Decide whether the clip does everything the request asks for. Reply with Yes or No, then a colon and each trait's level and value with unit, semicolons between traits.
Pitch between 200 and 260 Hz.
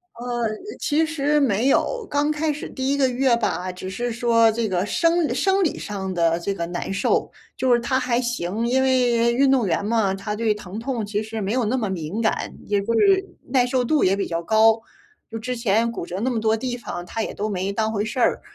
Yes: high, 230 Hz